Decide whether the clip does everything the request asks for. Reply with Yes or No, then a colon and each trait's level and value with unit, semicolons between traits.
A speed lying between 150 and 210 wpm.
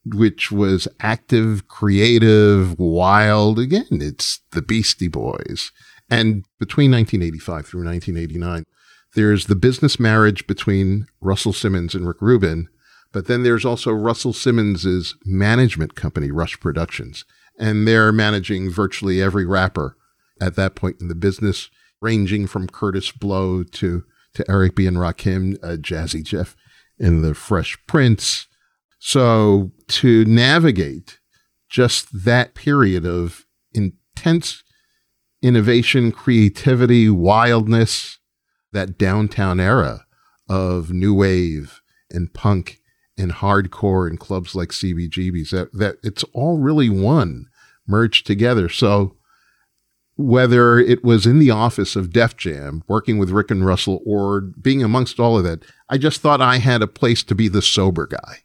No: slow, 135 wpm